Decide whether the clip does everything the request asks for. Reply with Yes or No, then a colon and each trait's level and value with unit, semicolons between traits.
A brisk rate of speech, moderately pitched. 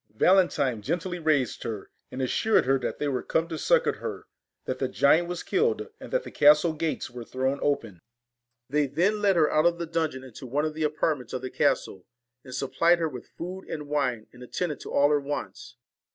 Yes: fast, 240 wpm; medium, 150 Hz